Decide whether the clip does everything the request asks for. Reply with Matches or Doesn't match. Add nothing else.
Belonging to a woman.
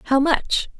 Matches